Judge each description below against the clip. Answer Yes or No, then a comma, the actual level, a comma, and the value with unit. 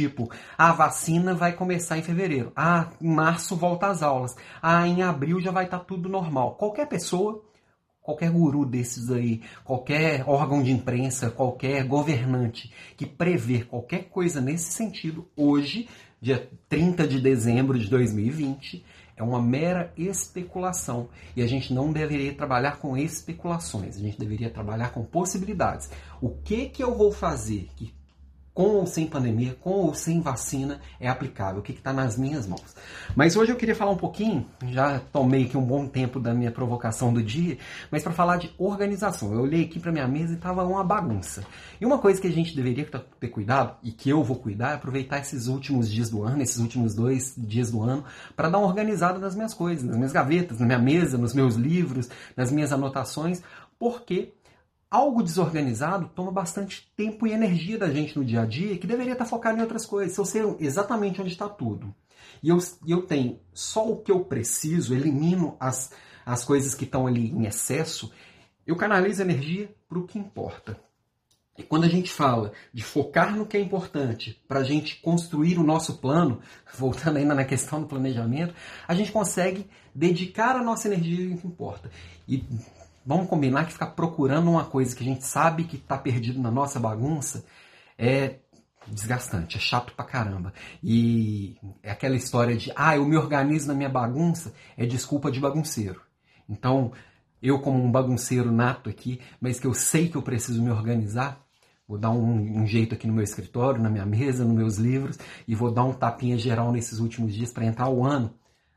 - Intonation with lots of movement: Yes, wide, 6.0 semitones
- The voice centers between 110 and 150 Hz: Yes, medium, 140 Hz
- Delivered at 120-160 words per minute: No, fast, 185 wpm